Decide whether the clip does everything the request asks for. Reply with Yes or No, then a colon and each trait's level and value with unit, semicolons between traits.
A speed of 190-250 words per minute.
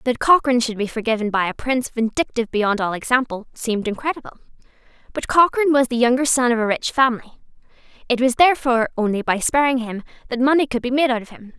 Yes: average, 200 wpm